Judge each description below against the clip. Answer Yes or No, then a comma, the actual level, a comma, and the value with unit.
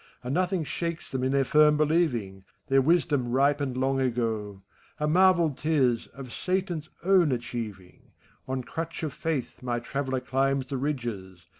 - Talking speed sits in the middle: Yes, average, 160 wpm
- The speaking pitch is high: No, low, 135 Hz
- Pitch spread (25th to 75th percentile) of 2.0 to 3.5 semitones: No, average, 4.3 semitones